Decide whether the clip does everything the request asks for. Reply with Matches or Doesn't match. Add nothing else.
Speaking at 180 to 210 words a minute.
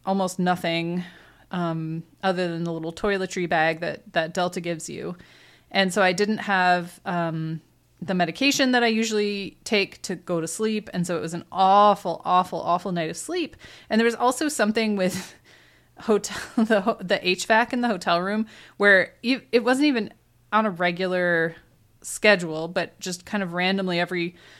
Doesn't match